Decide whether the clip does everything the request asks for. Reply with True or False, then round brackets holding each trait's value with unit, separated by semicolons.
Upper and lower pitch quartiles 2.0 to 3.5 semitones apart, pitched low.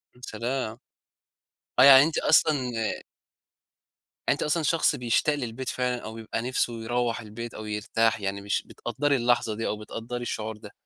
True (2.7 semitones; 120 Hz)